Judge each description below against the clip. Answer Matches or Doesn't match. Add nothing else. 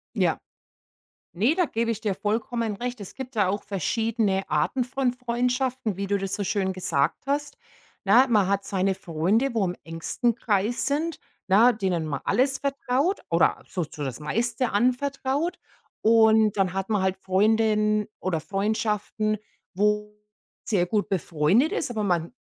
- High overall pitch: Matches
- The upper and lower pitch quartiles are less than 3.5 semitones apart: Doesn't match